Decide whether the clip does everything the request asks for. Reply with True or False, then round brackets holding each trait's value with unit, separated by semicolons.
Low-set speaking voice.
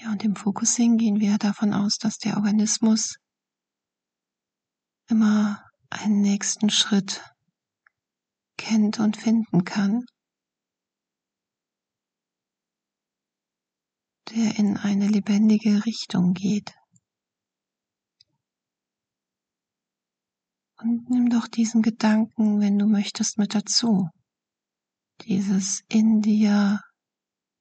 False (210 Hz)